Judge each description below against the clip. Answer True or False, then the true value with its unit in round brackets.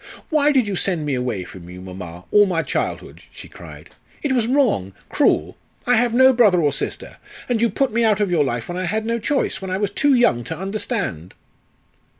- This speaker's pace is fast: True (215 wpm)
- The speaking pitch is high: True (200 Hz)